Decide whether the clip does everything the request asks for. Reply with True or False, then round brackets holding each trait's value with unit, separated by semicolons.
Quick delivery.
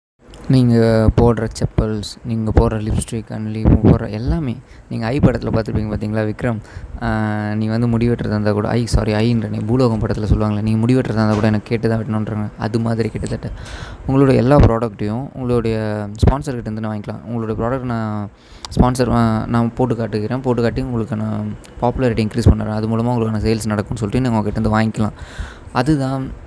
True (160 wpm)